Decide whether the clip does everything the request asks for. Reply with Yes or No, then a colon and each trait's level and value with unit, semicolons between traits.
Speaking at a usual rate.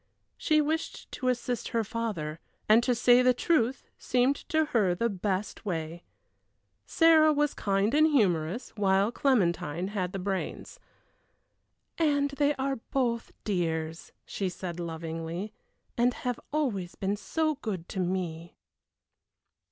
No: slow, 130 wpm